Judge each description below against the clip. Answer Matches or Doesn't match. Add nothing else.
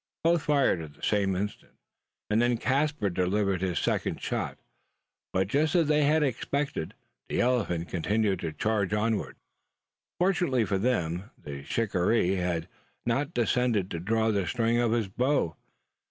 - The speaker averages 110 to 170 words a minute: Matches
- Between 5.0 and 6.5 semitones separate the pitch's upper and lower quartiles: Matches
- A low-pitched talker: Matches